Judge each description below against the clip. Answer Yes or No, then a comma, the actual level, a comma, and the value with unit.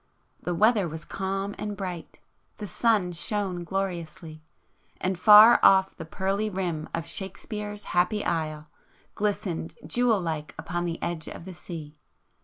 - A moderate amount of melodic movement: Yes, average, 3.7 semitones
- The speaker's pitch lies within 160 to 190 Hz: Yes, medium, 185 Hz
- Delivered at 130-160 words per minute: Yes, slow, 135 wpm